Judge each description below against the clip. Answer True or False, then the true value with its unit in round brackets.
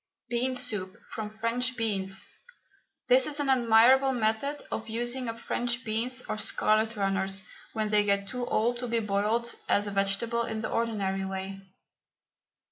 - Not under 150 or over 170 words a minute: True (155 wpm)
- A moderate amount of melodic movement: True (3.0 semitones)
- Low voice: False (225 Hz)